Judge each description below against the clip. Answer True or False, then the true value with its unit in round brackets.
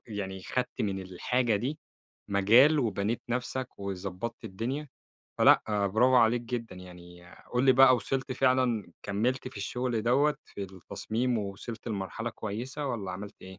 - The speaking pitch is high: False (115 Hz)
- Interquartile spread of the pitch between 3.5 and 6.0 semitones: True (4.3 semitones)